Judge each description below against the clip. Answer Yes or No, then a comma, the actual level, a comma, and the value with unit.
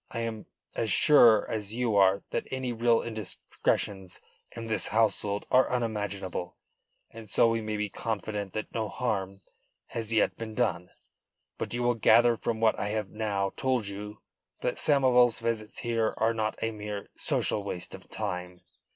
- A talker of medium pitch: No, low, 110 Hz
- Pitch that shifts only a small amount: Yes, narrow, 2.3 semitones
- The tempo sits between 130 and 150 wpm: No, average, 165 wpm